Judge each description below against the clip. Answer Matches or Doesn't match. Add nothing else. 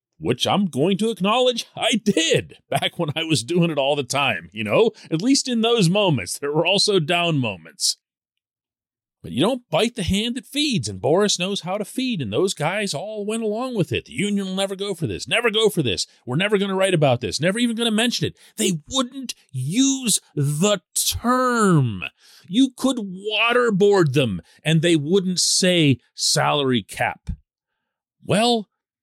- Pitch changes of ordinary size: Doesn't match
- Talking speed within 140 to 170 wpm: Doesn't match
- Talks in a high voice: Matches